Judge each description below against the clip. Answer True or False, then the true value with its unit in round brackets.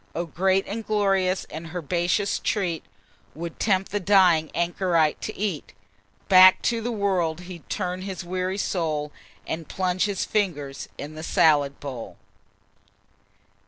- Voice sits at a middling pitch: True (180 Hz)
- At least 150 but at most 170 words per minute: False (135 wpm)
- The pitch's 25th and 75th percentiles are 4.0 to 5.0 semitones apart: False (3.2 semitones)